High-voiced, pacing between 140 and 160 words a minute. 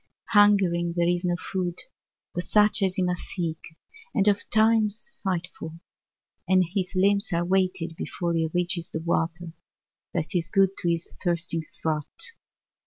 No: medium, 180 Hz; average, 150 wpm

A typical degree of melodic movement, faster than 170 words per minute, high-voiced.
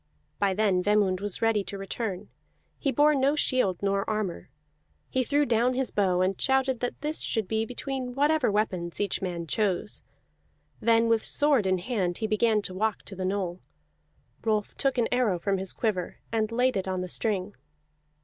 Yes: average, 4.5 semitones; average, 180 wpm; high, 215 Hz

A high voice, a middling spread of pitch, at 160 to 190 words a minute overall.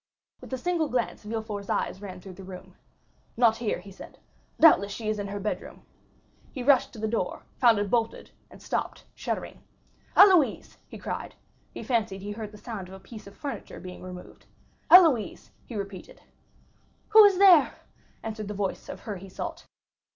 Yes: high, 215 Hz; average, 4.0 semitones; average, 180 wpm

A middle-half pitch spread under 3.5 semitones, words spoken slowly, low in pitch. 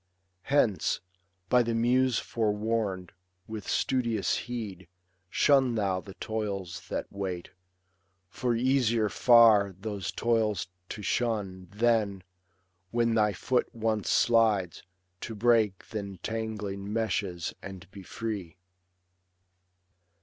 Yes: average, 2.9 semitones; slow, 105 wpm; low, 110 Hz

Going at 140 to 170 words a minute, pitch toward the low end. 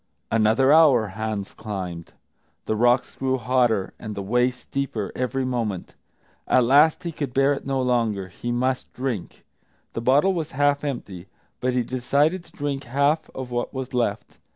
Yes: average, 165 wpm; low, 125 Hz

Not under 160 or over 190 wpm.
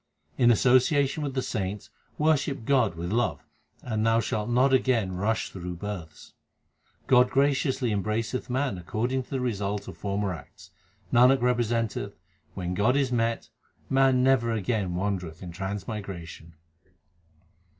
No: average, 140 wpm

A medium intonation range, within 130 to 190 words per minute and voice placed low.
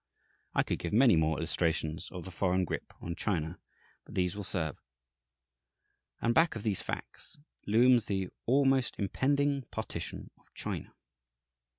No: wide, 6.4 semitones; average, 145 wpm; low, 100 Hz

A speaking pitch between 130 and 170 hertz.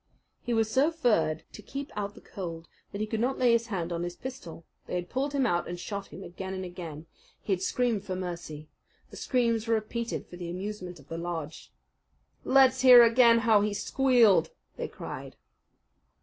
No: high, 205 Hz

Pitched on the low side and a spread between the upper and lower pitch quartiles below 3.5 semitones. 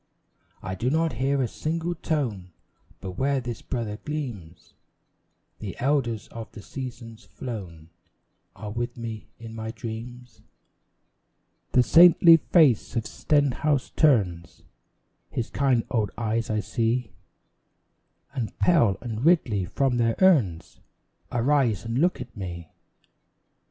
No: low, 120 Hz; average, 4.4 semitones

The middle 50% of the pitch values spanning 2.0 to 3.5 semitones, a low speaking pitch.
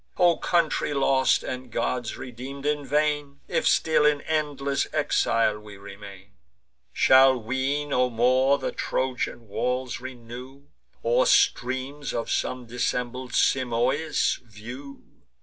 Yes: average, 2.8 semitones; low, 130 Hz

